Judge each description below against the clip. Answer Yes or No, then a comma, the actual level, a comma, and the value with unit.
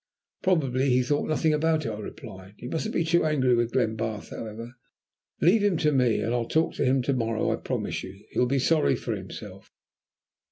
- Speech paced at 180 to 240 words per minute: Yes, average, 200 wpm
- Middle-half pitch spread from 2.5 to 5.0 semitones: No, wide, 5.4 semitones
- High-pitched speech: No, low, 130 Hz